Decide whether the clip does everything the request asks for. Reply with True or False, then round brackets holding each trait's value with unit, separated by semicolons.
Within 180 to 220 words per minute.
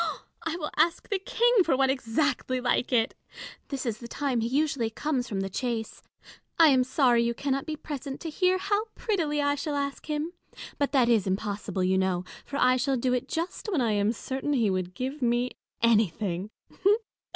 True (195 wpm)